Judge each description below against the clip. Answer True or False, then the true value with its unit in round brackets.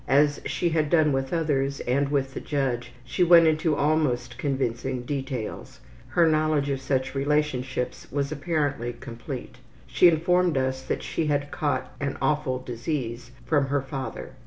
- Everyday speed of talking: True (155 wpm)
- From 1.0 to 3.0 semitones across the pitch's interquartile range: True (2.7 semitones)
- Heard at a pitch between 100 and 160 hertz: True (140 Hz)